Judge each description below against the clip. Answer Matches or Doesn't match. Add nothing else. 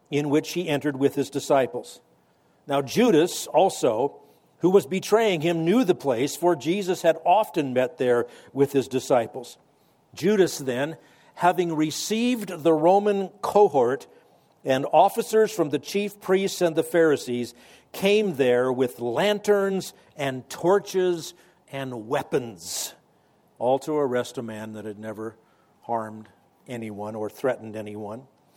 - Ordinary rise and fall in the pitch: Doesn't match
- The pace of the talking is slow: Matches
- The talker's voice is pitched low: Doesn't match